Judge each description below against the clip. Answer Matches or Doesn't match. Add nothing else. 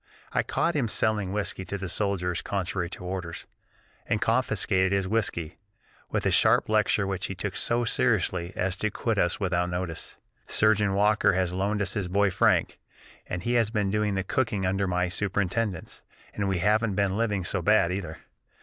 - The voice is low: Matches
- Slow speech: Doesn't match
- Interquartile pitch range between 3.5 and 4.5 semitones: Doesn't match